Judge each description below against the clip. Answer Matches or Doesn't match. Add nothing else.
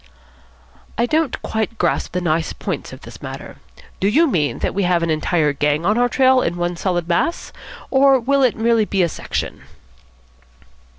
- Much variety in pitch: Matches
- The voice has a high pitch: Matches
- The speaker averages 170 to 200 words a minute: Matches